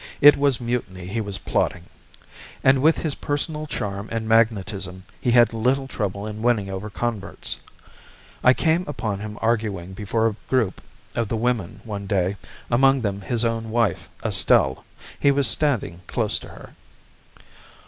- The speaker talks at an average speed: Yes, average, 155 wpm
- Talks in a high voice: No, low, 110 Hz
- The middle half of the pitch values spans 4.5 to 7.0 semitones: No, average, 3.8 semitones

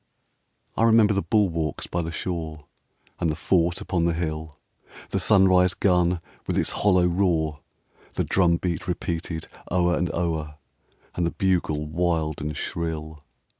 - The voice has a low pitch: Yes, very low, 85 Hz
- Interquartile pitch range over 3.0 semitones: No, narrow, 2.4 semitones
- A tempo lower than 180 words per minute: Yes, average, 145 wpm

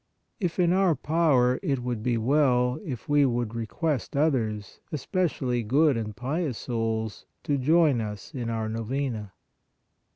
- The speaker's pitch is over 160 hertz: No, low, 125 Hz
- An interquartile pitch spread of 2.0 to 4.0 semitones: No, average, 4.8 semitones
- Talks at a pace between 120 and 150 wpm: Yes, average, 140 wpm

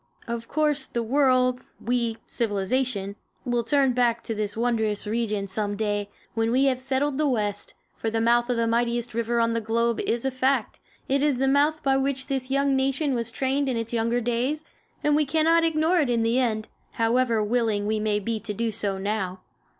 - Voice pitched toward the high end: Yes, high, 235 Hz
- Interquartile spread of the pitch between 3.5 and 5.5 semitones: No, average, 3.1 semitones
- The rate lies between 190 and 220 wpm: Yes, average, 200 wpm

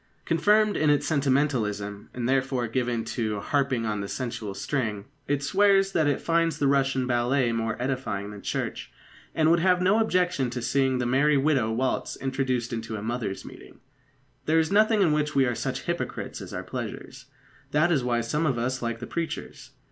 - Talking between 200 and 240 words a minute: No, average, 185 wpm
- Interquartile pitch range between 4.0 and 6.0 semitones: Yes, average, 4.6 semitones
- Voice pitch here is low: Yes, low, 130 Hz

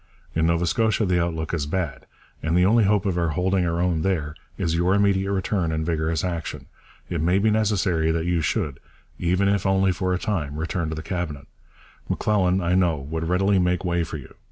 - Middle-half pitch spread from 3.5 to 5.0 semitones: No, average, 2.8 semitones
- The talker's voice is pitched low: Yes, very low, 90 Hz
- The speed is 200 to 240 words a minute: Yes, fast, 205 wpm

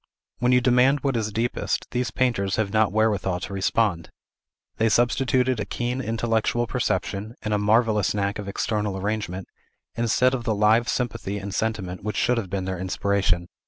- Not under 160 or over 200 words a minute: Yes, average, 170 wpm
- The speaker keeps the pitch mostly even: No, average, 3.2 semitones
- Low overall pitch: Yes, low, 110 Hz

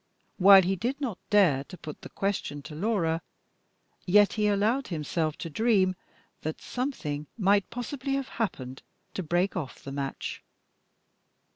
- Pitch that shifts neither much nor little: No, wide, 5.8 semitones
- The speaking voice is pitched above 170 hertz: Yes, high, 190 Hz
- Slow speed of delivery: No, average, 145 wpm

